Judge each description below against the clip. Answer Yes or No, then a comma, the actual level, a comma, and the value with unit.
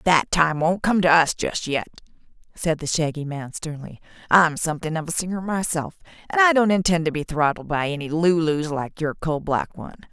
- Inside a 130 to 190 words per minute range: No, average, 200 wpm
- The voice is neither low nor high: Yes, medium, 165 Hz